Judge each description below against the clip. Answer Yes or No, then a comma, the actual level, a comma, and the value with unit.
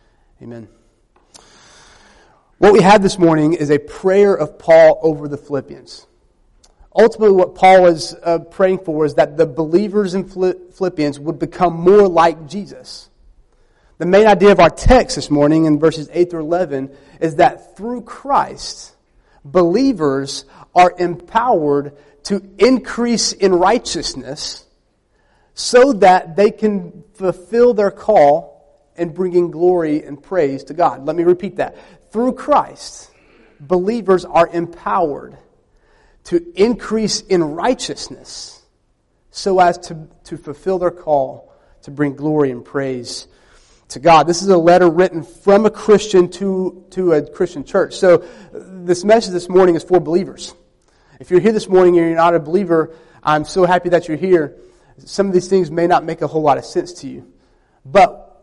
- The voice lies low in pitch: No, medium, 175 Hz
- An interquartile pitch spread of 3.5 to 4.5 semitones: Yes, average, 4.0 semitones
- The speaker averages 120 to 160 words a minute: Yes, average, 155 wpm